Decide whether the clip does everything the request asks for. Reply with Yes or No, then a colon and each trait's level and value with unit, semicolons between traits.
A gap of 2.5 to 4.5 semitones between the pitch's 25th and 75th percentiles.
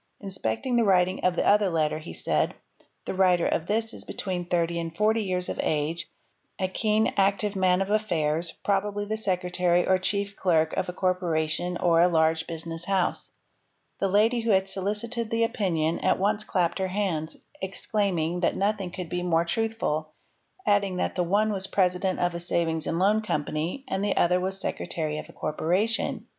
Yes: average, 3.2 semitones